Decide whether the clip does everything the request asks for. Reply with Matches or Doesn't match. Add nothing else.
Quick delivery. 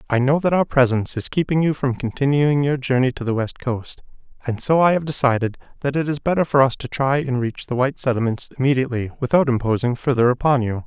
Matches